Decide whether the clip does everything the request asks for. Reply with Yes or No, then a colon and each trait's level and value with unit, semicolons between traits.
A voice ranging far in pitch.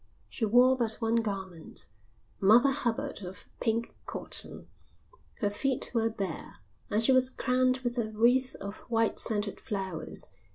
No: average, 3.5 semitones